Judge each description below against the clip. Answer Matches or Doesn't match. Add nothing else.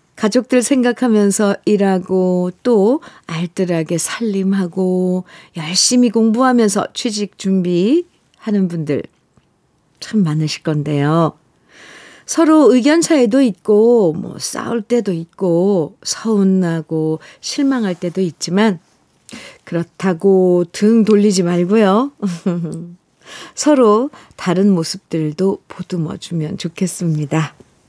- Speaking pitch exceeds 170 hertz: Matches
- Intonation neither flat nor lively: Matches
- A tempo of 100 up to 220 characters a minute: Matches